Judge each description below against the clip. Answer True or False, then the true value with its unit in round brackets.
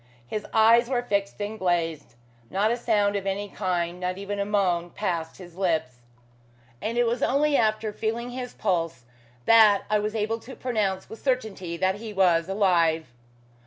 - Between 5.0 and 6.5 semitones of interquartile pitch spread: False (3.9 semitones)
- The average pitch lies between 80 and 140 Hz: False (200 Hz)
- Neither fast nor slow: True (170 wpm)